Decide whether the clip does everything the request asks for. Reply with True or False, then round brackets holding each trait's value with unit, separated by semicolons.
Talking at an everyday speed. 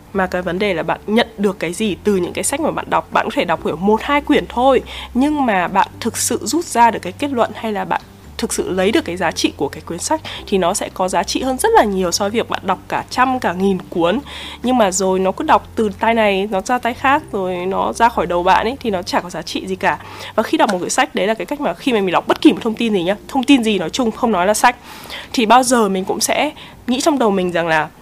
False (305 wpm)